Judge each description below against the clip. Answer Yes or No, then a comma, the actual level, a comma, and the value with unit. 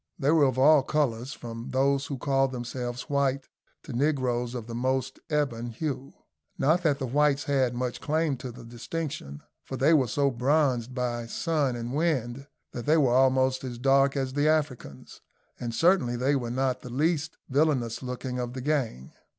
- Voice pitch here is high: No, low, 130 Hz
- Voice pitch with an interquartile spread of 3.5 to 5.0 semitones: No, average, 2.9 semitones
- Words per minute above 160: Yes, average, 180 wpm